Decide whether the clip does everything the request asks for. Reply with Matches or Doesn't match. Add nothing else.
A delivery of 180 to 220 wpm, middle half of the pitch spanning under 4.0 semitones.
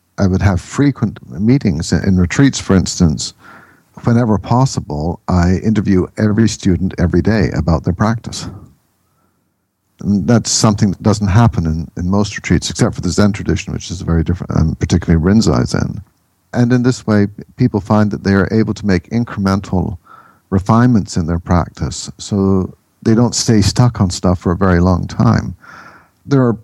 Doesn't match